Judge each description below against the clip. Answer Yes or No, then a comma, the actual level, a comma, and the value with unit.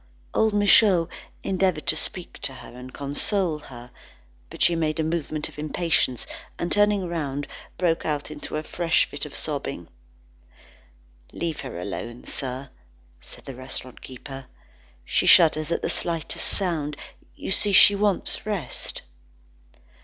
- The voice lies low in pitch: No, medium, 155 Hz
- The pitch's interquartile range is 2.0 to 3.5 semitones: No, average, 4.7 semitones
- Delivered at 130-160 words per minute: Yes, average, 140 wpm